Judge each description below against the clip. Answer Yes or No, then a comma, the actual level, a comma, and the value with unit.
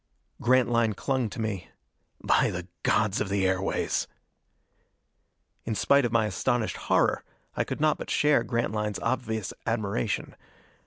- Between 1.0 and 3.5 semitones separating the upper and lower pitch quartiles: Yes, average, 2.9 semitones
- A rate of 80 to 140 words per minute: Yes, slow, 135 wpm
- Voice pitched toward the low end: Yes, low, 110 Hz